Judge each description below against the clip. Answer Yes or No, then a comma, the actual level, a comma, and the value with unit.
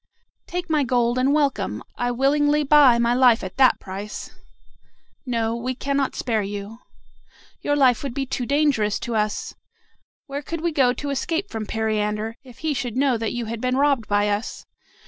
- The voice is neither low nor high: No, very high, 250 Hz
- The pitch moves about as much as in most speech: Yes, average, 4.1 semitones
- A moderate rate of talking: Yes, average, 185 wpm